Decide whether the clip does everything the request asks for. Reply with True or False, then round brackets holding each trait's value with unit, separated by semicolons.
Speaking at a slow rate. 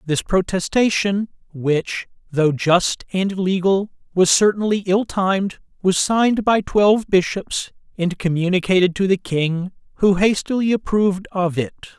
True (130 wpm)